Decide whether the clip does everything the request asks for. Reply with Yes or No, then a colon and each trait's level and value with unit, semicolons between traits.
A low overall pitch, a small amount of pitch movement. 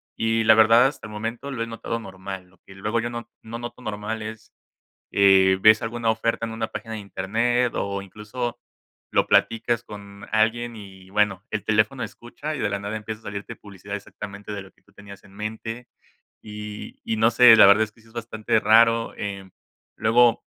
Yes: low, 110 Hz; narrow, 2.3 semitones